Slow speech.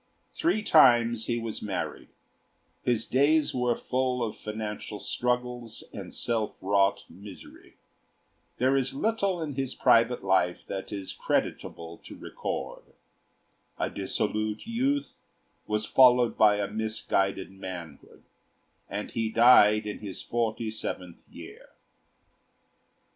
Yes: slow, 115 wpm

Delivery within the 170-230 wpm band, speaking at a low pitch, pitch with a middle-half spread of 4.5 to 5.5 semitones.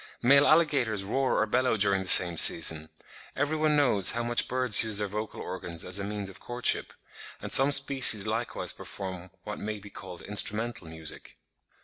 Yes: average, 175 wpm; low, 105 Hz; average, 4.8 semitones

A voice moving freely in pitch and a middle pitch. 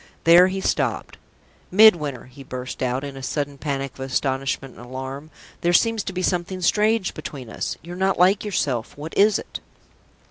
Yes: wide, 5.8 semitones; medium, 150 Hz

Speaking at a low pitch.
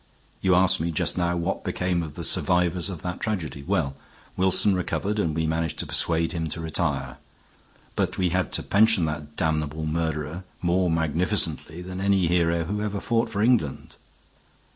Yes: very low, 85 Hz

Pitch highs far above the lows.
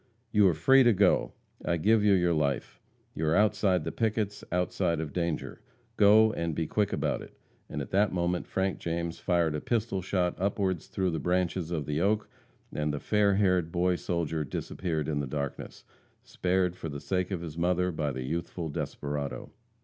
No: average, 3.4 semitones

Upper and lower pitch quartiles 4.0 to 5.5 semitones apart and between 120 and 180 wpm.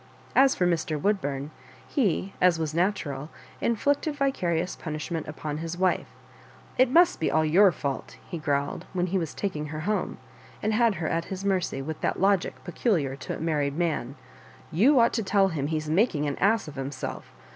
No: average, 4.8 semitones; average, 190 wpm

